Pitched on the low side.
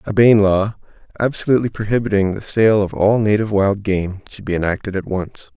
Yes: low, 105 Hz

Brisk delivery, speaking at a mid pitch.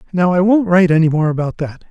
Yes: fast, 250 wpm; medium, 175 Hz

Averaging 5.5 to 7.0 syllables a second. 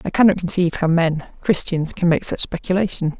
Yes: 5.8 syllables/s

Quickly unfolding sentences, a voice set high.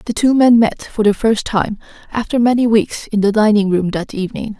Yes: fast, 220 wpm; high, 215 Hz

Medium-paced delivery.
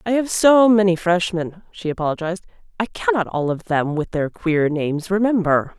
Yes: average, 175 wpm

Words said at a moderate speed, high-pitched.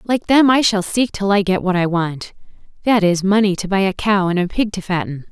No: fast, 250 wpm; high, 195 Hz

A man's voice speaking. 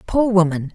No: female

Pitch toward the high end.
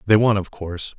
No: low, 100 Hz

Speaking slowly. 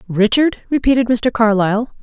Yes: slow, 120 wpm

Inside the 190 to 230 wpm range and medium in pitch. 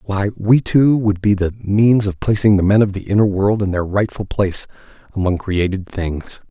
No: fast, 205 wpm; low, 100 Hz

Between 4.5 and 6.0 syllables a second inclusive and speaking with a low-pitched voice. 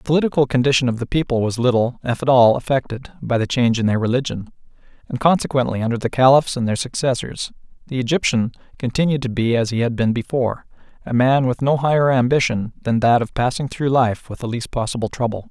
No: 6.2 syllables/s; low, 125 Hz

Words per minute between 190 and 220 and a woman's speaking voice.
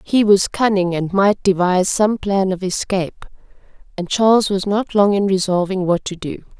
No: average, 180 wpm; female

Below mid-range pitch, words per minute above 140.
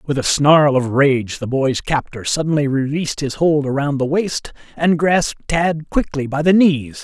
No: medium, 145 Hz; average, 190 wpm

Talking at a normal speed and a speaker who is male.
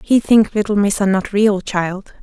No: average, 190 wpm; female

